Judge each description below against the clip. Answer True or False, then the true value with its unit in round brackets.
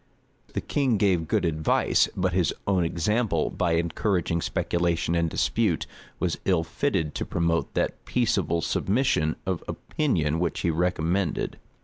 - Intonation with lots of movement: False (2.8 semitones)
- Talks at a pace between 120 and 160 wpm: True (140 wpm)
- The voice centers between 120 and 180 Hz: False (85 Hz)